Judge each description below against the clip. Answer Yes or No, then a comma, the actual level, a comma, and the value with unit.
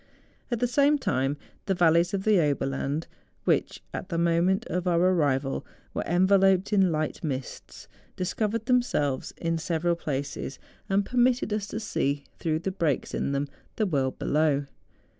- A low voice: No, medium, 170 Hz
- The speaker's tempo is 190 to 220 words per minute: No, average, 155 wpm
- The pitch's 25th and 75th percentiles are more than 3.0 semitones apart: Yes, wide, 5.4 semitones